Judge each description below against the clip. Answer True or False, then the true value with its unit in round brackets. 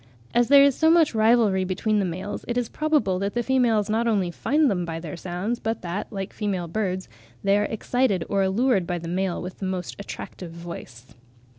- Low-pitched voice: False (200 Hz)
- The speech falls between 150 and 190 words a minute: False (205 wpm)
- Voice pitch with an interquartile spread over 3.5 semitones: True (4.6 semitones)